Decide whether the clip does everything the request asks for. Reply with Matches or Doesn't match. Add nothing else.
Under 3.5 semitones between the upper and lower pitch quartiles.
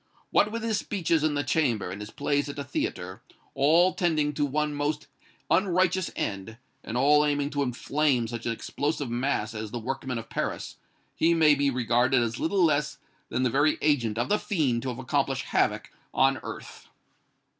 Doesn't match